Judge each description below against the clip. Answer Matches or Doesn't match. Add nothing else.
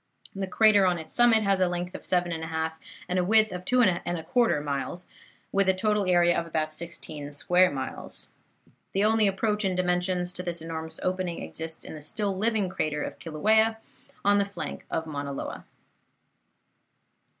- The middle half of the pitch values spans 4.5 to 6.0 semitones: Doesn't match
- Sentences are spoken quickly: Doesn't match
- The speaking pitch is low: Doesn't match